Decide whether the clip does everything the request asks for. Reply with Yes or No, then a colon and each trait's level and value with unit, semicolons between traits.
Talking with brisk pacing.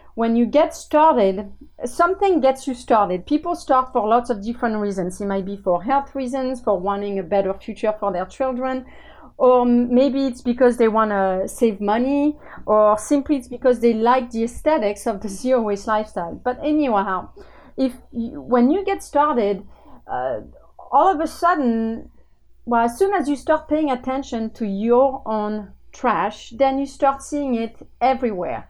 No: average, 170 wpm